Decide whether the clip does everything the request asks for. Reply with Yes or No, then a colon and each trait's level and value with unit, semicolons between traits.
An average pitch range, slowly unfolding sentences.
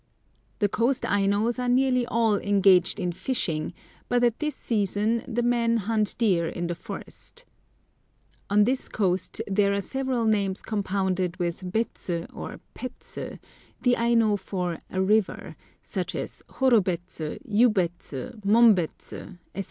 Yes: average, 4.1 semitones; slow, 130 wpm